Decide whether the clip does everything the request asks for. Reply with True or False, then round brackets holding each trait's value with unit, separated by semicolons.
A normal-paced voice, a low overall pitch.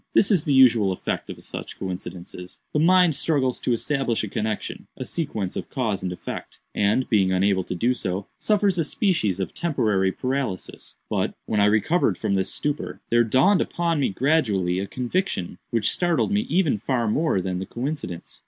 True (175 wpm; 120 Hz)